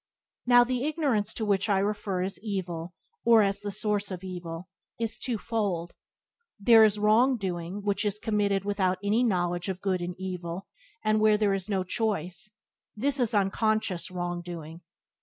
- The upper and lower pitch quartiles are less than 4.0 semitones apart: Yes, average, 3.0 semitones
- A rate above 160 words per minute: Yes, average, 175 wpm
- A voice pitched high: Yes, high, 200 Hz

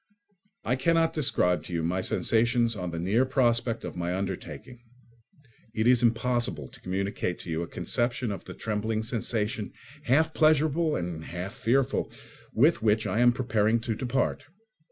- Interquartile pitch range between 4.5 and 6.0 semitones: Yes, average, 4.8 semitones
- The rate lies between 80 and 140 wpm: No, average, 155 wpm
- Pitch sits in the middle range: No, low, 115 Hz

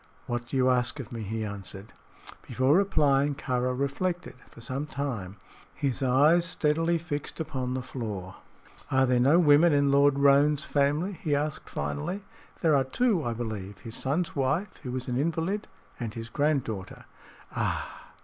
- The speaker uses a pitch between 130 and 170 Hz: Yes, low, 135 Hz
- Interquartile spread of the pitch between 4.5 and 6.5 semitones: No, average, 3.9 semitones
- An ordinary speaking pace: Yes, average, 160 wpm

